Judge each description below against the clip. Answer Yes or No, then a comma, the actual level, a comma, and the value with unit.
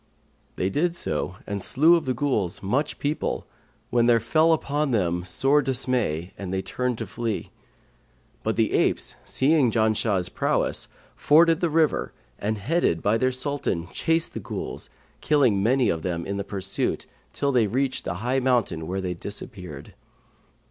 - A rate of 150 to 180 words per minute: Yes, average, 160 wpm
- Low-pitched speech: Yes, low, 120 Hz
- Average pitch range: No, wide, 6.6 semitones